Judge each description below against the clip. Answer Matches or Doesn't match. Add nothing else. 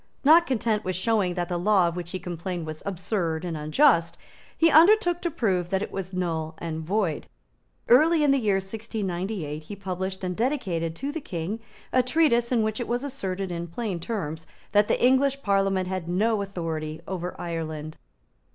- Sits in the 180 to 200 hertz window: Matches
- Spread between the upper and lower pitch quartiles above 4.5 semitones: Matches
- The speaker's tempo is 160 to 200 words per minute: Matches